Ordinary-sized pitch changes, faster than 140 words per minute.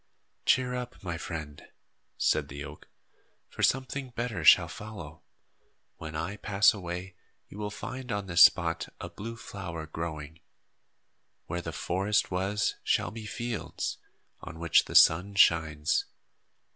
No: average, 4.7 semitones; slow, 135 wpm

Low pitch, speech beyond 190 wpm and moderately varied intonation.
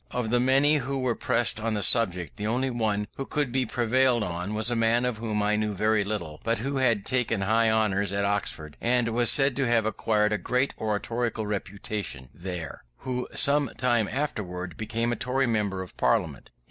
Yes: low, 110 Hz; average, 200 wpm; average, 3.2 semitones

